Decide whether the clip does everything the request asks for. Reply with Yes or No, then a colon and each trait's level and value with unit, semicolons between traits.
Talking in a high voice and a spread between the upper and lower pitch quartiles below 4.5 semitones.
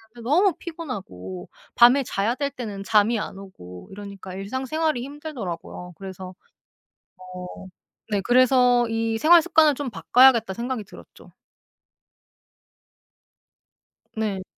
No: high, 225 Hz; wide, 5.6 semitones